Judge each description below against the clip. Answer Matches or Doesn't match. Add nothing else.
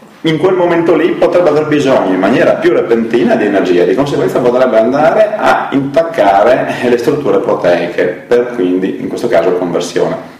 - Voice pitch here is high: Doesn't match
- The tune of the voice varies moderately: Doesn't match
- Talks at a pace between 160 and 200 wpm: Matches